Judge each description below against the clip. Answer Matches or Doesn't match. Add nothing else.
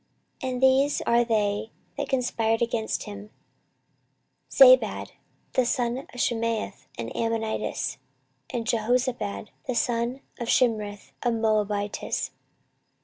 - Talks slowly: Matches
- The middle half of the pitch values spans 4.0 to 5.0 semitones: Doesn't match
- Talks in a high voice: Matches